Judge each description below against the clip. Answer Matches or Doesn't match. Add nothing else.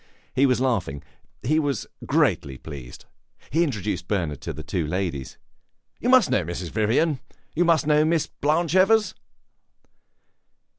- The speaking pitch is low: Matches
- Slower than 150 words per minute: Matches